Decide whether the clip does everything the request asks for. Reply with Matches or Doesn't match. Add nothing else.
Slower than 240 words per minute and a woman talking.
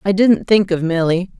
Matches